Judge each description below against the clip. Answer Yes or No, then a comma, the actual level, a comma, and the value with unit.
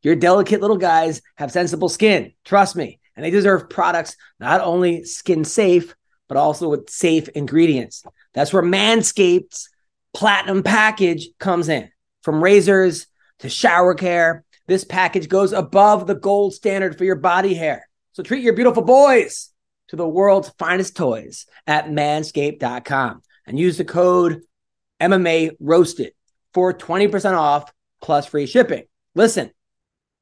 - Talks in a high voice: No, medium, 180 Hz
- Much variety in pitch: No, average, 3.3 semitones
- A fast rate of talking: No, average, 140 wpm